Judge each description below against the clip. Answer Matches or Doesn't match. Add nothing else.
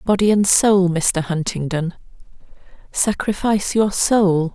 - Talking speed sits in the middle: Doesn't match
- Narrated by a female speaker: Matches